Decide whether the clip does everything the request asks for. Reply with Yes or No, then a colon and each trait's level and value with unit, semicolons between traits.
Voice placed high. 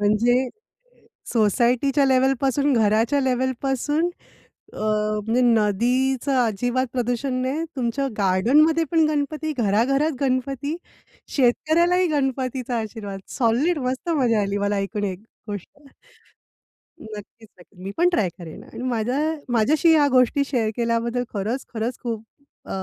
Yes: high, 245 Hz